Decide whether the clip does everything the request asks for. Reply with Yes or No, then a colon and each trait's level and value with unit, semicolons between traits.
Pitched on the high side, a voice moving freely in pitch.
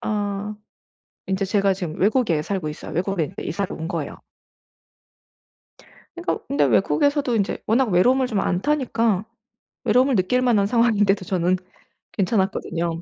No: high, 200 Hz; average, 4.5 semitones